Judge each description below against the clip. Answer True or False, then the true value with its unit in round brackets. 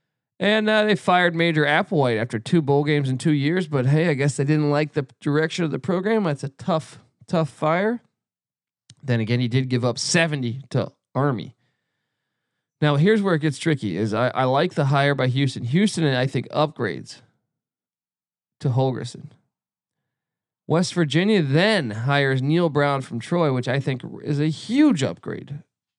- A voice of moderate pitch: True (150 Hz)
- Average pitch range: True (4.1 semitones)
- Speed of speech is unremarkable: True (175 wpm)